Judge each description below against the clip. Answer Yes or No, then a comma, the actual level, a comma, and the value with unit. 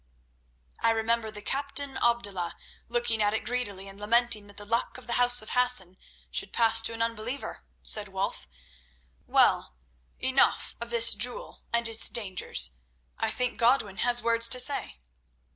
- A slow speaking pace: No, average, 160 wpm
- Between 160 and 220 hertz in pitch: No, high, 230 Hz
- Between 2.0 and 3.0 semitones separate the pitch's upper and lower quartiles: Yes, average, 2.7 semitones